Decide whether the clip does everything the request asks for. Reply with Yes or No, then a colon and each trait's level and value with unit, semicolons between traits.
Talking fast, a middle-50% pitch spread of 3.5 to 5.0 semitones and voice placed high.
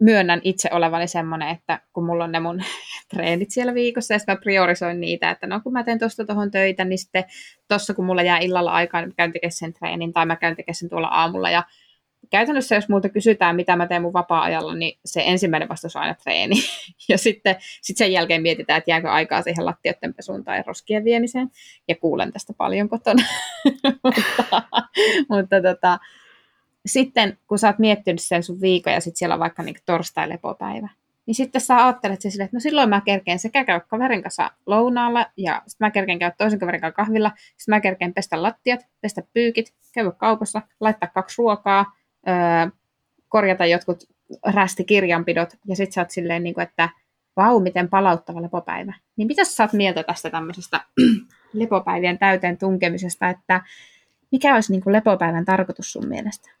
Yes: fast, 175 wpm; average, 4.0 semitones; high, 195 Hz